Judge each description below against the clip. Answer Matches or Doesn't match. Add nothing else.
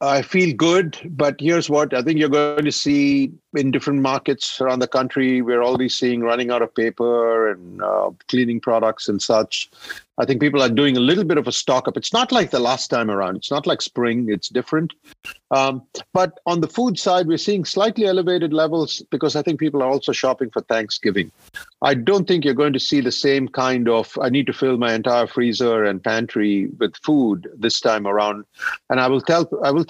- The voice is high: Doesn't match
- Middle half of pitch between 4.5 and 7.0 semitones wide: Matches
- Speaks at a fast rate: Matches